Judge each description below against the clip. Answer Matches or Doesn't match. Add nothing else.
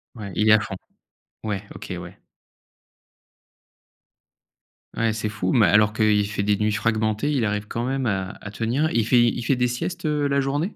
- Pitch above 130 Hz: Doesn't match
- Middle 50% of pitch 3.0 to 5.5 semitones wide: Matches